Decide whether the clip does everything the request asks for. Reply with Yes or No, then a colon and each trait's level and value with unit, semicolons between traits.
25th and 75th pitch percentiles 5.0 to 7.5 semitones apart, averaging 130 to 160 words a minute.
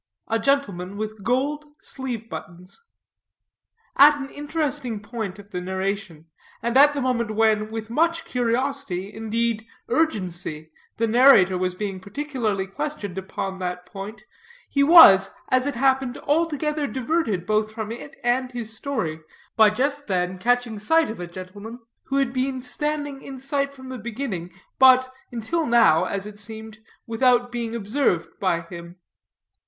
Yes: wide, 5.5 semitones; average, 150 wpm